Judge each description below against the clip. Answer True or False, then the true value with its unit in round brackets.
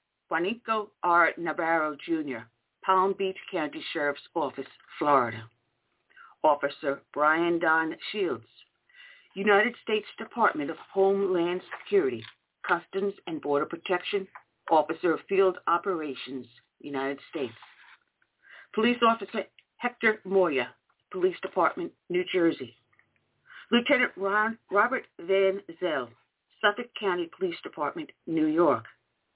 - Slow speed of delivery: True (100 wpm)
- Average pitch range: False (5.9 semitones)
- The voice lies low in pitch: False (190 Hz)